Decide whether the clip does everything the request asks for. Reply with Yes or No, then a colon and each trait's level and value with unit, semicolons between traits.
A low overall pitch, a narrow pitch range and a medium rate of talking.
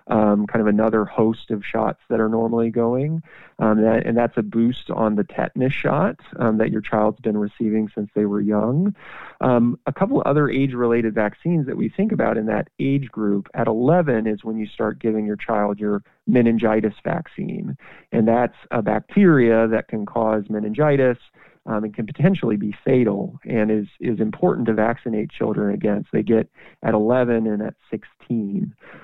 Yes: low, 110 Hz; narrow, 2.0 semitones; average, 185 wpm